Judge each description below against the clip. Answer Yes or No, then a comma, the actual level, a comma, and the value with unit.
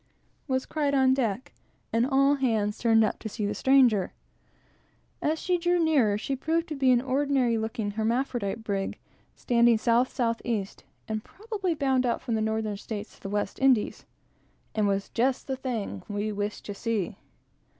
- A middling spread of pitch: Yes, average, 3.9 semitones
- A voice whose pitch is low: No, high, 235 Hz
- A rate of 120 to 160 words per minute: No, average, 170 wpm